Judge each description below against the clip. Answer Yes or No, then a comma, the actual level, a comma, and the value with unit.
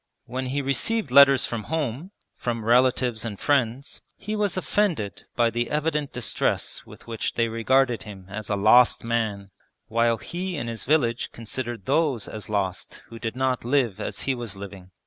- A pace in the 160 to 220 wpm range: Yes, average, 170 wpm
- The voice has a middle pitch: No, low, 120 Hz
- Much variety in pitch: No, average, 3.8 semitones